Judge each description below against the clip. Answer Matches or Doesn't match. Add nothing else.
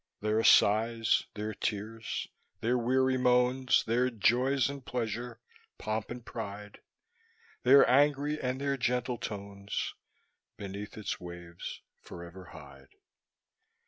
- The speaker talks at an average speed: Doesn't match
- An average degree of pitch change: Matches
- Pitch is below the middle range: Matches